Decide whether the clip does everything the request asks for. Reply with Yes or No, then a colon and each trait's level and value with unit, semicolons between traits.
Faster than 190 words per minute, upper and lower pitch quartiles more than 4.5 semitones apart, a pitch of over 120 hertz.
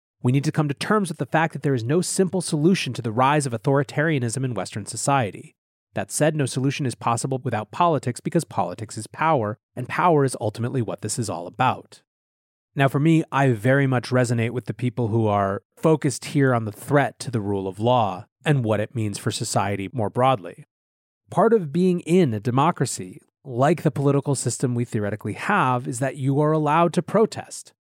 Yes: average, 200 wpm; average, 5.0 semitones; low, 130 Hz